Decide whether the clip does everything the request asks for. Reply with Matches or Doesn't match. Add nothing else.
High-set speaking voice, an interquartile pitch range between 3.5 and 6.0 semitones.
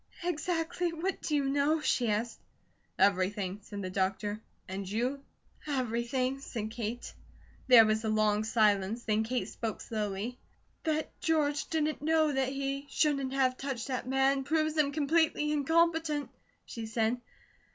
Matches